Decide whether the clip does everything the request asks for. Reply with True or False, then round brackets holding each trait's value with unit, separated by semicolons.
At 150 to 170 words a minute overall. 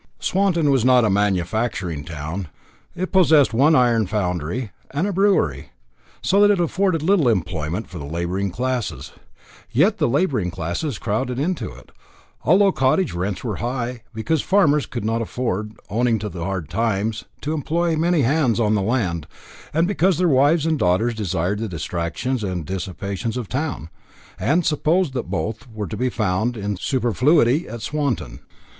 True (165 wpm)